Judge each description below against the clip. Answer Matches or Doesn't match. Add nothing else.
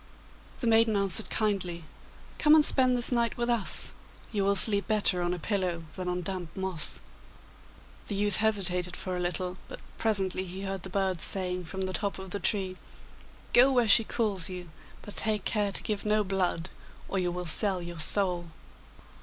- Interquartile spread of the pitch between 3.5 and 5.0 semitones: Doesn't match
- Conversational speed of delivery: Matches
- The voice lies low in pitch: Doesn't match